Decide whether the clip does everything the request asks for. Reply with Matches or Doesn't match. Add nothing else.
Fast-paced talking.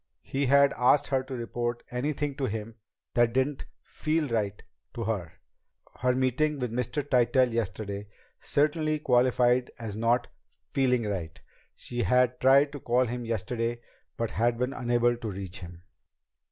Doesn't match